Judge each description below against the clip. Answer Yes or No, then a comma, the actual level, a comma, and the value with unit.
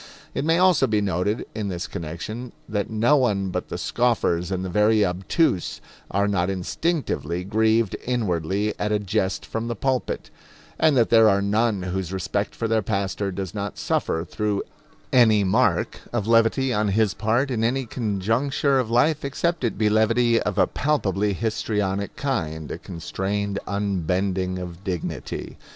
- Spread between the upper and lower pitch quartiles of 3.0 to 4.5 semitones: Yes, average, 3.6 semitones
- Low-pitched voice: Yes, low, 105 Hz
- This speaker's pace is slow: No, average, 160 wpm